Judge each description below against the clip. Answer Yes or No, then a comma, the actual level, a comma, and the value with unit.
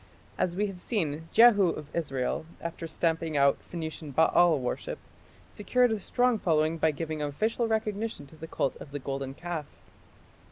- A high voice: No, medium, 165 Hz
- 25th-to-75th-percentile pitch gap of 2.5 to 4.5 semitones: No, wide, 5.4 semitones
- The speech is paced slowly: No, average, 160 wpm